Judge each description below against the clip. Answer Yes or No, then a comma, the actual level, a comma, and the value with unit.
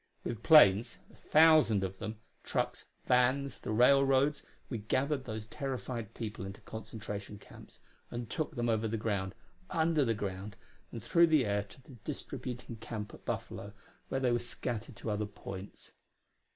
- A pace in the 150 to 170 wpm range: Yes, average, 160 wpm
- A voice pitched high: No, low, 115 Hz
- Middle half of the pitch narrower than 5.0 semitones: Yes, average, 4.2 semitones